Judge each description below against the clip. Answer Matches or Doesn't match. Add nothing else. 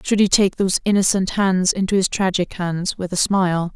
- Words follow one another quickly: Matches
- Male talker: Doesn't match